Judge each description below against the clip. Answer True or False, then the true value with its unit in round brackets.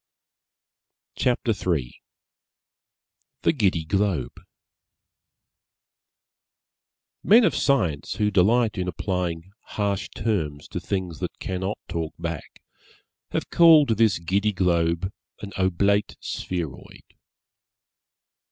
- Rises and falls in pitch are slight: False (3.9 semitones)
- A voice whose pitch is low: True (95 Hz)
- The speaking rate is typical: False (90 wpm)